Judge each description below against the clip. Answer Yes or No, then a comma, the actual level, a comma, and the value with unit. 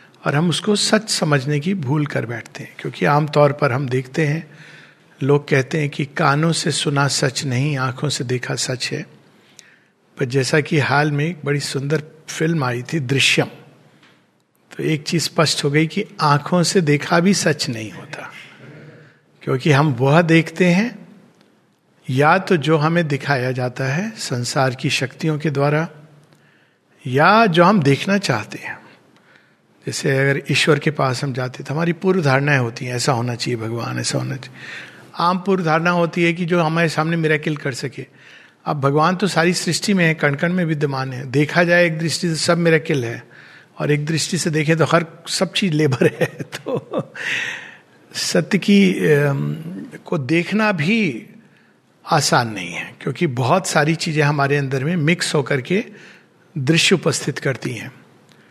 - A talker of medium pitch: Yes, medium, 155 Hz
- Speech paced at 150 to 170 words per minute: Yes, average, 165 wpm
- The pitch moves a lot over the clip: No, average, 3.5 semitones